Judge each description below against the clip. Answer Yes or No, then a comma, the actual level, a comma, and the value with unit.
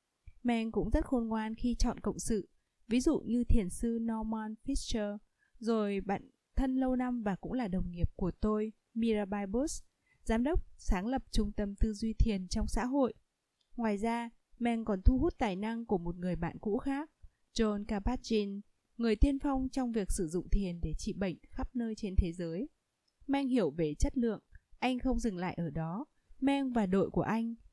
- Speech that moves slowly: No, average, 195 wpm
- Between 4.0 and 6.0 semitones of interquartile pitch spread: No, average, 3.5 semitones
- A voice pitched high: Yes, high, 225 Hz